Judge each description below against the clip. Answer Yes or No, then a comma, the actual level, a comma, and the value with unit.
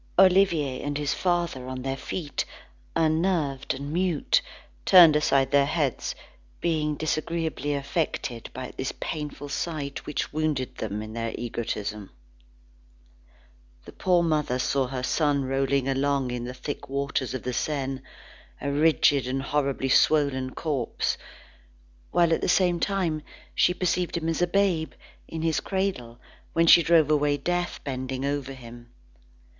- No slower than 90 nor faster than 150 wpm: Yes, average, 140 wpm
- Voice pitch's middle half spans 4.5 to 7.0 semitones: No, average, 3.8 semitones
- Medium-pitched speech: Yes, medium, 145 Hz